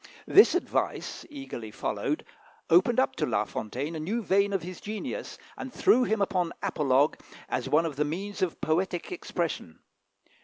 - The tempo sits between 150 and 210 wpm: Yes, average, 160 wpm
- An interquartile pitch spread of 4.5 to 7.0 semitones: Yes, average, 4.9 semitones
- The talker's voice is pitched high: No, medium, 180 Hz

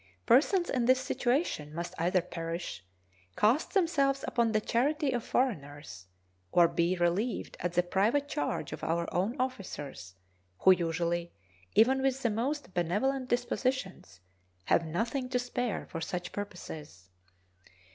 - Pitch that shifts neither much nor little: No, wide, 7.2 semitones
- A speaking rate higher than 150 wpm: No, slow, 135 wpm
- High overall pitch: Yes, high, 205 Hz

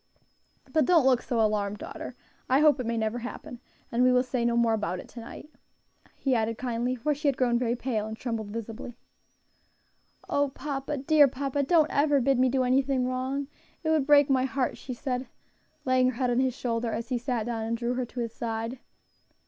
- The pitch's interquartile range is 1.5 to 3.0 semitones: Yes, average, 2.7 semitones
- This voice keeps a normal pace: No, fast, 210 wpm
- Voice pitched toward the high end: Yes, very high, 250 Hz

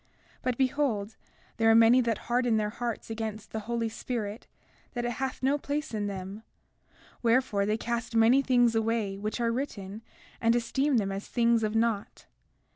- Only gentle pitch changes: Yes, narrow, 2.2 semitones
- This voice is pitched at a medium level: No, high, 230 Hz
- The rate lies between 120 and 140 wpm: No, average, 175 wpm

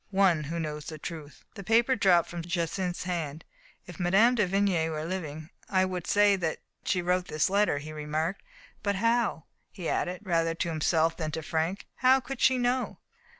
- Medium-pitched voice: Yes, medium, 175 Hz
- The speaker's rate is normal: Yes, average, 185 wpm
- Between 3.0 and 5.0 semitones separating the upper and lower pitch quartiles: Yes, average, 3.8 semitones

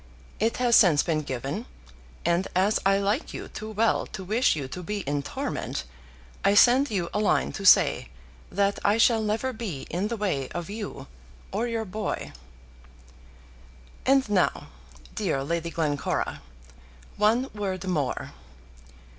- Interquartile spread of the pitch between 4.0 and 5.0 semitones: Yes, average, 4.4 semitones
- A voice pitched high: Yes, high, 200 Hz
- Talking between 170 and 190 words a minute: No, average, 145 wpm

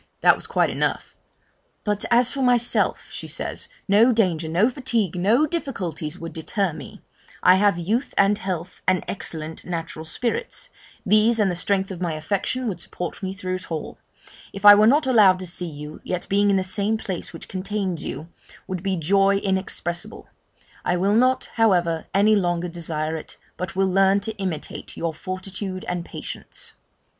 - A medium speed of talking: Yes, average, 175 wpm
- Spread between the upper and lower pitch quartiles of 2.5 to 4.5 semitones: Yes, average, 3.3 semitones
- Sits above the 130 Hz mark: Yes, high, 190 Hz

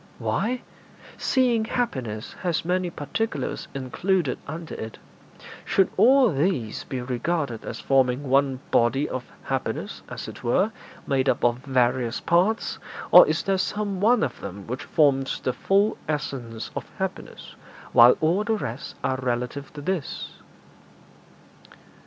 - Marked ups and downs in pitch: Yes, wide, 7.2 semitones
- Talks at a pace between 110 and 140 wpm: Yes, slow, 135 wpm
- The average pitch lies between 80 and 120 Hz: No, medium, 140 Hz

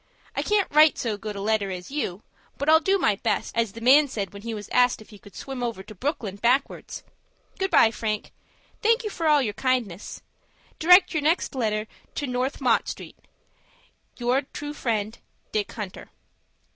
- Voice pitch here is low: No, high, 240 Hz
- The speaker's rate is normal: Yes, average, 190 wpm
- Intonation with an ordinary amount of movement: No, wide, 5.7 semitones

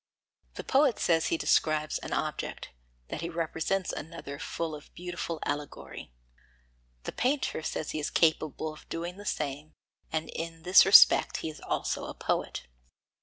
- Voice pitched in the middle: Yes, medium, 165 Hz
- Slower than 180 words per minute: Yes, average, 155 wpm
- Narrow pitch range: Yes, narrow, 2.2 semitones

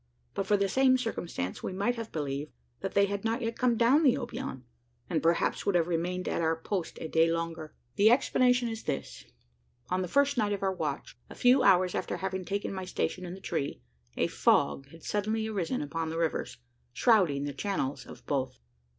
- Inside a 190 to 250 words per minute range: Yes, average, 200 wpm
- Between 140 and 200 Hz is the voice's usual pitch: Yes, high, 190 Hz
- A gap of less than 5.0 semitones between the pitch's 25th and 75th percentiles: No, wide, 5.4 semitones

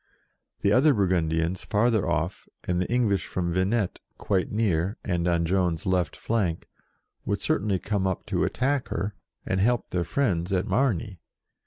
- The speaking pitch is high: No, very low, 95 Hz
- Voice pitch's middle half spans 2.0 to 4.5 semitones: Yes, average, 3.8 semitones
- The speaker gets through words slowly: No, average, 155 wpm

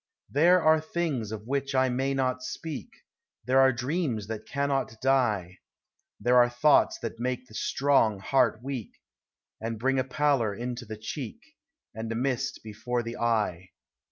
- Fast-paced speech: No, average, 155 wpm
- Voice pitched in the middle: No, low, 125 Hz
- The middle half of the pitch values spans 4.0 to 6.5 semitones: No, average, 3.4 semitones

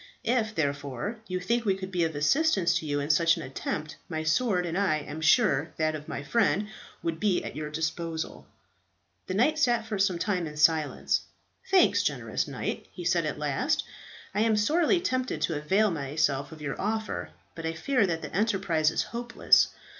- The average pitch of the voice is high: No, medium, 175 Hz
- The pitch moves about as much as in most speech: No, wide, 5.8 semitones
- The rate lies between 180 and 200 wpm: Yes, average, 190 wpm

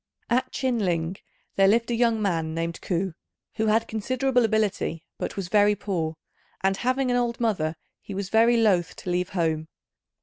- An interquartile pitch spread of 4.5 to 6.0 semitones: Yes, average, 4.8 semitones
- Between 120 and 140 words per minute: No, average, 175 wpm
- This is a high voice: Yes, high, 205 Hz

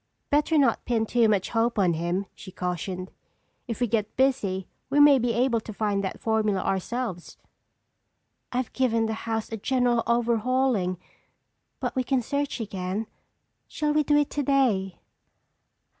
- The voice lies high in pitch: Yes, high, 230 Hz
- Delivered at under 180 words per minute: Yes, average, 150 wpm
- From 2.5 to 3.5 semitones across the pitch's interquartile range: No, average, 4.6 semitones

